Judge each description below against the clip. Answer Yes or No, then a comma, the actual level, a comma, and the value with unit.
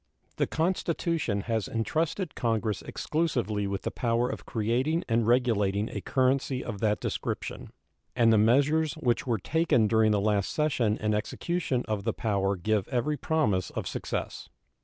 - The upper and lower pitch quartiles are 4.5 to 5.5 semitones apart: Yes, average, 5.1 semitones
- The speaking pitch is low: Yes, low, 115 Hz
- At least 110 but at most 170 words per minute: Yes, average, 155 wpm